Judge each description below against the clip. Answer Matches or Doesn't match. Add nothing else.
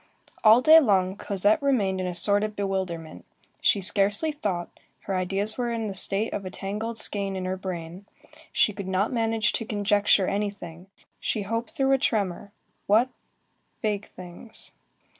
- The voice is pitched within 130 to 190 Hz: Doesn't match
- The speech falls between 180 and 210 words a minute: Doesn't match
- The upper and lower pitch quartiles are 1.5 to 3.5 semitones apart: Matches